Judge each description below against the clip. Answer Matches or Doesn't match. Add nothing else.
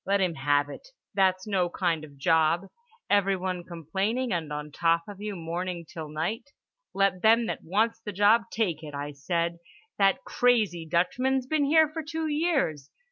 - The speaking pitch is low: Doesn't match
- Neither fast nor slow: Matches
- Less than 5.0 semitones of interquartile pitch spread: Doesn't match